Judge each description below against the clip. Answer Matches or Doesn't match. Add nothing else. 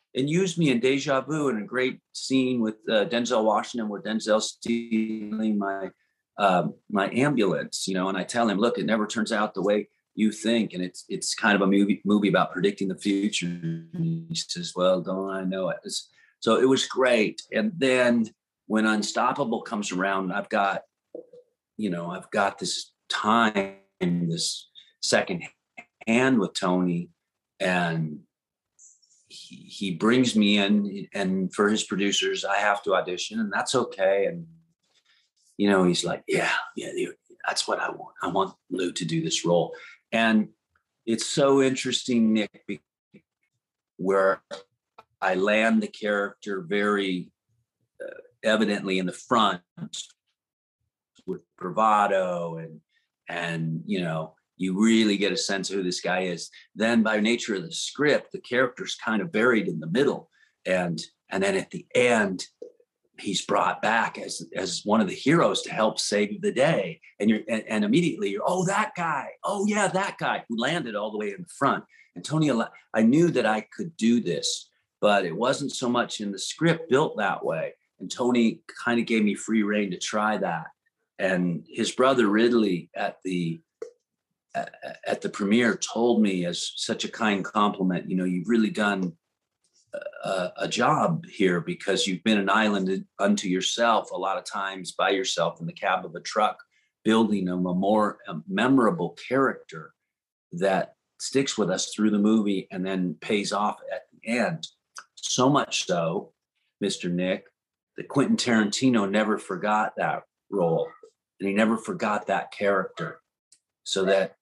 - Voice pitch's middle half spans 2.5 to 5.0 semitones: Doesn't match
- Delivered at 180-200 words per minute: Doesn't match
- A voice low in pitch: Matches